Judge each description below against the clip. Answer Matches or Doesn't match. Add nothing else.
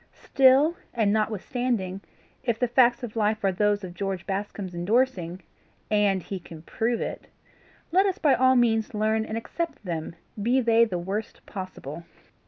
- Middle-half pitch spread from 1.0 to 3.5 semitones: Doesn't match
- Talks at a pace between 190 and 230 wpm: Doesn't match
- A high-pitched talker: Matches